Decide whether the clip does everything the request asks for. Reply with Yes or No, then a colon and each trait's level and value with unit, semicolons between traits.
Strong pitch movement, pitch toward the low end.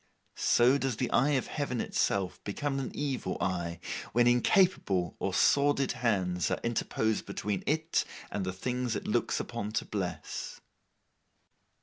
Yes: wide, 5.8 semitones; low, 120 Hz